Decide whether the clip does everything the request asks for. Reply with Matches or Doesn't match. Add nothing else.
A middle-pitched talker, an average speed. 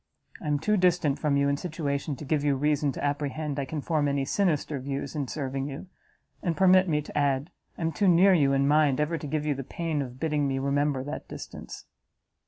Doesn't match